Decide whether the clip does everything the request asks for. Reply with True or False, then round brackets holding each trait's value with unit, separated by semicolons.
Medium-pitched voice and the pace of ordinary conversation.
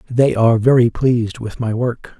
False (120 Hz; 190 wpm)